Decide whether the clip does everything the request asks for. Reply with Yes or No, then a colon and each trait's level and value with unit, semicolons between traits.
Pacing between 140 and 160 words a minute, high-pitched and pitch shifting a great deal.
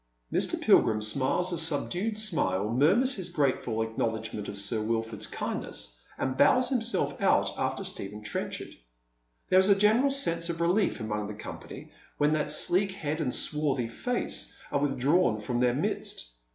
No: average, 155 wpm; medium, 145 Hz; wide, 8.6 semitones